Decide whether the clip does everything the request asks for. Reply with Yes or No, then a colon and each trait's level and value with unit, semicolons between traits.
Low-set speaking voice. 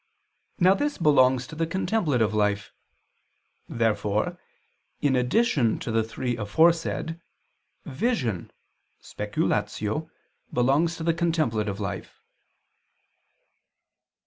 Yes: low, 130 Hz